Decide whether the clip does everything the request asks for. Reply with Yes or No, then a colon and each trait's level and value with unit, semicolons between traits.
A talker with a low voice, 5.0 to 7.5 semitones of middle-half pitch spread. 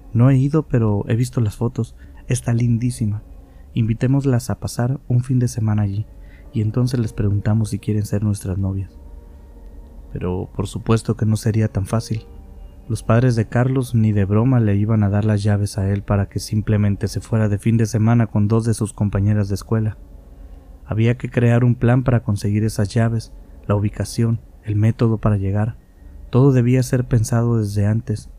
No: low, 110 Hz; narrow, 2.6 semitones